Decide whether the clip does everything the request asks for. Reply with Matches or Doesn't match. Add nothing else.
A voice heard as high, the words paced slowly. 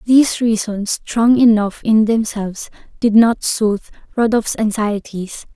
Matches